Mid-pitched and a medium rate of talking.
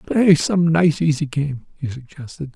Yes: medium, 150 Hz; average, 165 wpm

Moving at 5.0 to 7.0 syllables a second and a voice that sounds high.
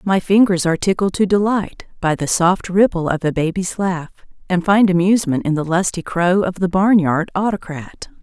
No: 5.1 syllables/s; medium, 180 Hz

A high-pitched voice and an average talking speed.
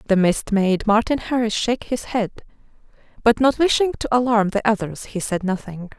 Yes: high, 220 Hz; average, 180 wpm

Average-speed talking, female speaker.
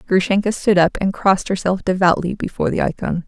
Yes: average, 185 wpm; female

